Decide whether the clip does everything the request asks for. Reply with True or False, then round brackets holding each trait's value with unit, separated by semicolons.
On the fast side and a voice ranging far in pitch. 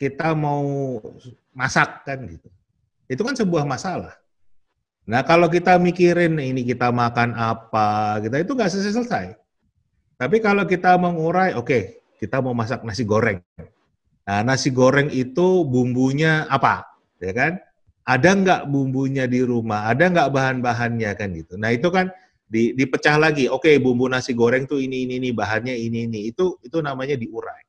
True (155 wpm; 5.8 semitones)